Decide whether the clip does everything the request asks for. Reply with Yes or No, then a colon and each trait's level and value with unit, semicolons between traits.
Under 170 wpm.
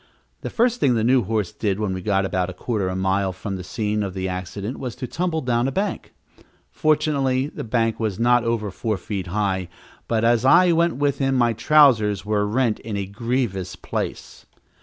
No: fast, 205 wpm